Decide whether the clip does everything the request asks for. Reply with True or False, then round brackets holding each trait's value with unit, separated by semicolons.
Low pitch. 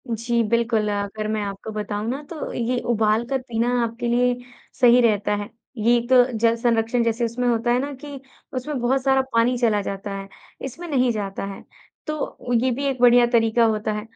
False (235 Hz)